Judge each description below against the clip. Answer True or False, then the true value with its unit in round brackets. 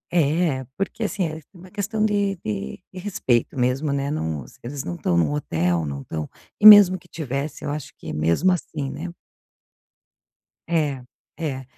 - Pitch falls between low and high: True (145 Hz)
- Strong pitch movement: True (7.2 semitones)